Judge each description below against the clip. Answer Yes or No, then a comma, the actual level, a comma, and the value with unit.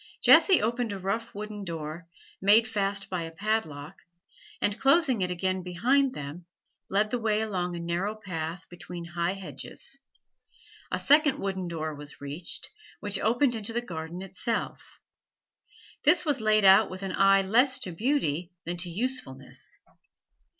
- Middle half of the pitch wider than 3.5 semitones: Yes, average, 4.5 semitones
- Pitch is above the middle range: Yes, high, 195 Hz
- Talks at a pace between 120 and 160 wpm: Yes, average, 150 wpm